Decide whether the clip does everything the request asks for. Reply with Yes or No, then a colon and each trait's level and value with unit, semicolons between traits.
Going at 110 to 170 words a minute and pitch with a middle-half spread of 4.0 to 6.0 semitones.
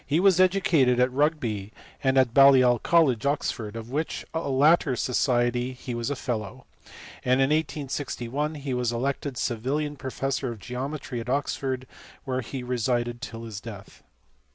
No: average, 150 wpm; average, 3.0 semitones